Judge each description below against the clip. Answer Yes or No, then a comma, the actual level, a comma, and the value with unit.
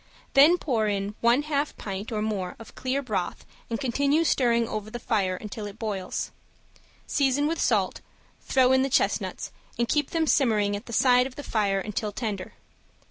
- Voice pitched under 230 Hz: No, high, 235 Hz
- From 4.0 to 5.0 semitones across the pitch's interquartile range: Yes, average, 4.6 semitones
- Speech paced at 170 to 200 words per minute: Yes, average, 180 wpm